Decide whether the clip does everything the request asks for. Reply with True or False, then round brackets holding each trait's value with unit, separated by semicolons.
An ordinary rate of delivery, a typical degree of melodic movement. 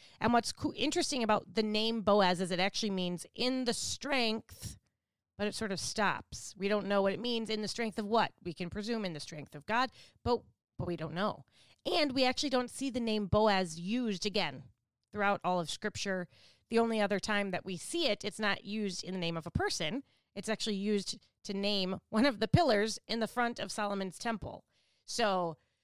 False (210 wpm; 3.3 semitones)